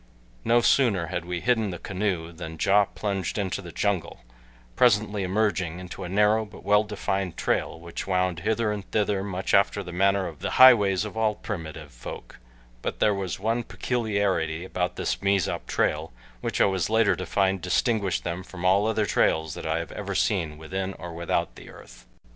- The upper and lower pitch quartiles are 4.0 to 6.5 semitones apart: No, average, 3.0 semitones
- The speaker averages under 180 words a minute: No, average, 185 wpm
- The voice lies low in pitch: Yes, very low, 95 Hz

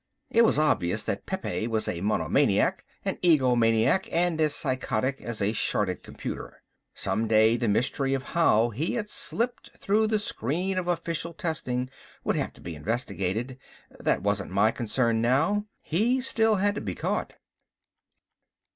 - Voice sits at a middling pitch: No, low, 130 Hz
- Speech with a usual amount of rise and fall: No, wide, 8.0 semitones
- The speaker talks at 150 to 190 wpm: Yes, average, 155 wpm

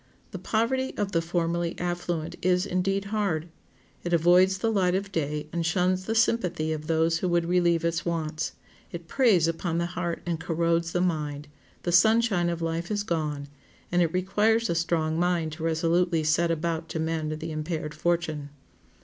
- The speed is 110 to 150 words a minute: No, average, 180 wpm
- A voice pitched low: No, medium, 170 Hz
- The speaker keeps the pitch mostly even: Yes, narrow, 1.9 semitones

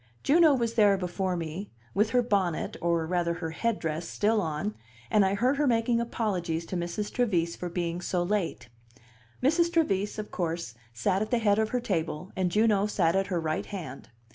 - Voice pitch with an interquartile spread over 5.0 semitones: No, average, 4.6 semitones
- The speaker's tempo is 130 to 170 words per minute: No, average, 190 wpm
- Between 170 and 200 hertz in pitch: Yes, high, 190 Hz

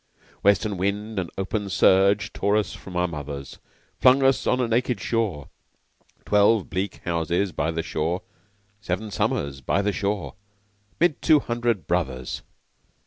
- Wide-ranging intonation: No, average, 4.2 semitones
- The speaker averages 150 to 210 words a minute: No, average, 140 wpm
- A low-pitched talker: Yes, low, 100 Hz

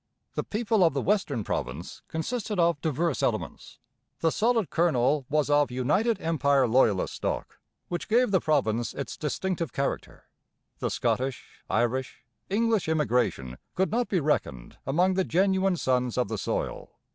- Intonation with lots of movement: Yes, wide, 6.8 semitones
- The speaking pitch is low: No, medium, 155 Hz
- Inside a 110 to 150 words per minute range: Yes, average, 145 wpm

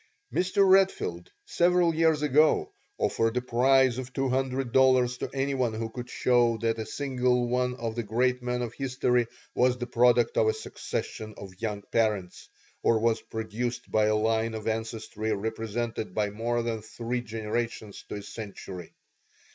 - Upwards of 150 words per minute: Yes, average, 165 wpm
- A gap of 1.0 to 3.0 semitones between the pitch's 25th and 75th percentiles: Yes, narrow, 2.4 semitones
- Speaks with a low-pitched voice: Yes, low, 120 Hz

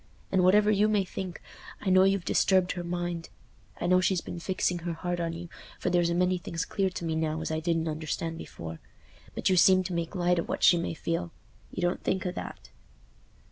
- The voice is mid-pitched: Yes, medium, 175 Hz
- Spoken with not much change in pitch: Yes, narrow, 1.9 semitones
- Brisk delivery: Yes, fast, 215 wpm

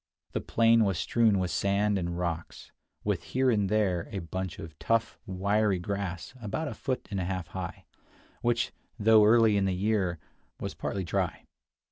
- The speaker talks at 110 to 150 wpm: No, average, 170 wpm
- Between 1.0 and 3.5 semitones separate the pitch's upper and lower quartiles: Yes, average, 3.2 semitones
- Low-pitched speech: Yes, low, 100 Hz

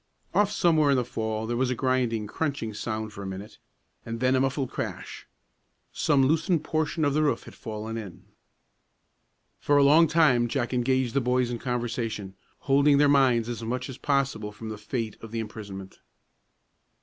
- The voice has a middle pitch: No, low, 125 Hz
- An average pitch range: Yes, average, 4.0 semitones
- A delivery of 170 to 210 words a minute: Yes, average, 175 wpm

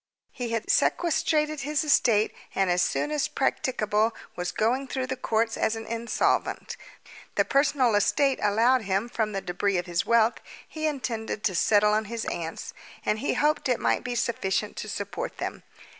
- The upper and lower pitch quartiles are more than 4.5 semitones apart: No, average, 4.1 semitones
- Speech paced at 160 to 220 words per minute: Yes, average, 175 wpm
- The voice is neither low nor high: No, high, 230 Hz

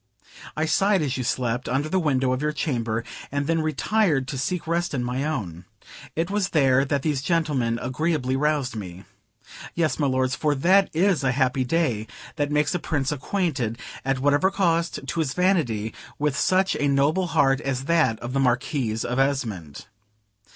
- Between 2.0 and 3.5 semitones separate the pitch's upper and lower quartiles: No, average, 4.1 semitones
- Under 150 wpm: No, average, 175 wpm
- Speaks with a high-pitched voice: No, medium, 140 Hz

